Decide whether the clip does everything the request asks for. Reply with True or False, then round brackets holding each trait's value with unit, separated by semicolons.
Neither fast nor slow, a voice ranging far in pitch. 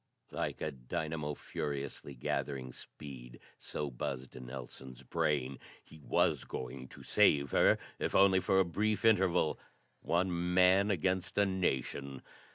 False (130 wpm; 5.8 semitones)